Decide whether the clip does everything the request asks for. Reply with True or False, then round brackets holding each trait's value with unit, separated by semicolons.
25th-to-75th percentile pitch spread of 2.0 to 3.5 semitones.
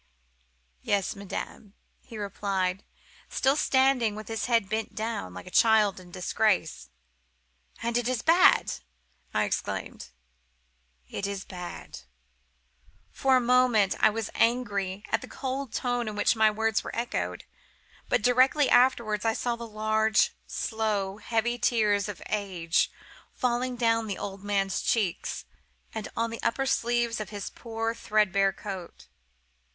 True (3.0 semitones)